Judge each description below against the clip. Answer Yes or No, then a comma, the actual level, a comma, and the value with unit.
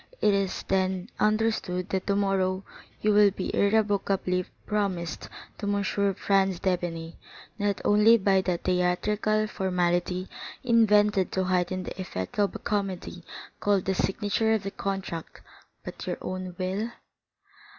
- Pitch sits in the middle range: No, high, 195 Hz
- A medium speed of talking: No, slow, 130 wpm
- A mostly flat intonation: Yes, narrow, 2.1 semitones